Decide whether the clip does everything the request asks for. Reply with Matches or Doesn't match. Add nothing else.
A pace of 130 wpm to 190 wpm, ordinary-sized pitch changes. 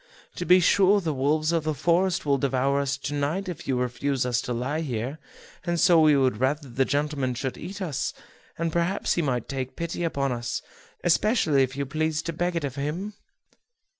Doesn't match